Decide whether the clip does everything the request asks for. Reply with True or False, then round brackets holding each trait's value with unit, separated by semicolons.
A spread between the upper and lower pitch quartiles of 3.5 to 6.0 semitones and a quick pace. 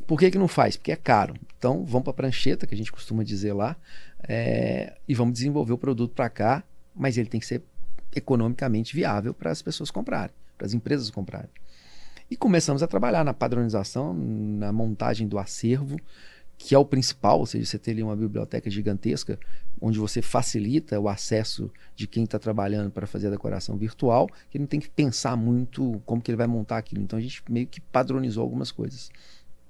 True (4.1 semitones; 200 wpm)